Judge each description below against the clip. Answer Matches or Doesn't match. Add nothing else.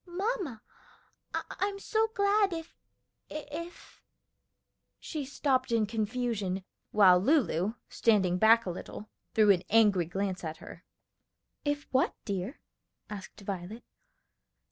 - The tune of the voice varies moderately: Doesn't match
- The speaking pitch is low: Doesn't match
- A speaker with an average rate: Doesn't match